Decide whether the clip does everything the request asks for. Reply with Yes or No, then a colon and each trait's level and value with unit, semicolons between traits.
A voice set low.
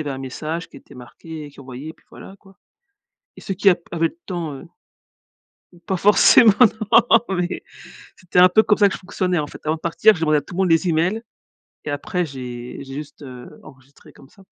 No: medium, 165 Hz